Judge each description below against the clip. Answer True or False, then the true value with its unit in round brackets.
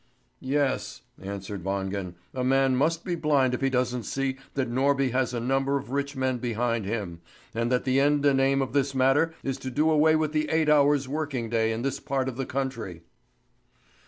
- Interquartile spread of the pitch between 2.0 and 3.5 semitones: True (2.8 semitones)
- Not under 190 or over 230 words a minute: True (200 wpm)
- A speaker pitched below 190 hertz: True (135 Hz)